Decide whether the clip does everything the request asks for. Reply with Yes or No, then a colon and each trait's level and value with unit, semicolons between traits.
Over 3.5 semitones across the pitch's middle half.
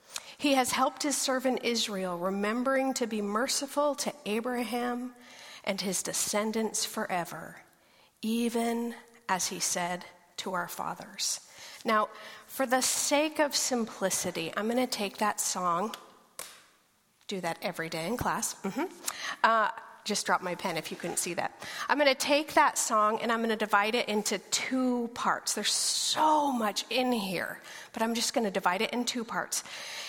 Yes: average, 4.3 semitones